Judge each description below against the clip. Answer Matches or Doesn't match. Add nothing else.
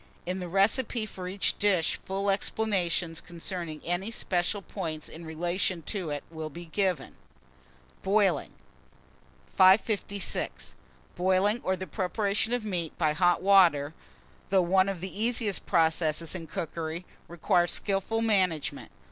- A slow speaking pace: Matches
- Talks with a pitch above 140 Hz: Matches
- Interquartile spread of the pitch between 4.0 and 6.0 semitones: Doesn't match